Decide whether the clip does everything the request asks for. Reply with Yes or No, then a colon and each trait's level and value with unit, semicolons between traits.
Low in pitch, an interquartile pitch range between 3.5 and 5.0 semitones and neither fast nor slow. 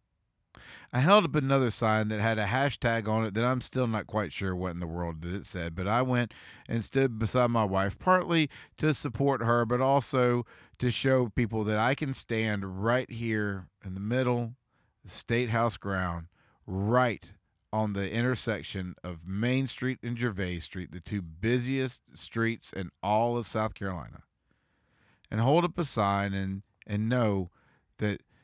Yes: low, 110 Hz; average, 4.2 semitones; average, 170 wpm